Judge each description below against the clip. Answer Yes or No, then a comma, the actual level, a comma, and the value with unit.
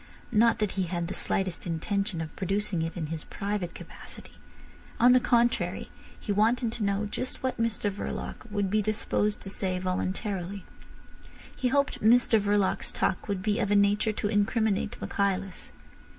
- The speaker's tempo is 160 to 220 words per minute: Yes, average, 165 wpm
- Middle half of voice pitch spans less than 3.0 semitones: Yes, narrow, 2.4 semitones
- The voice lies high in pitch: Yes, high, 205 Hz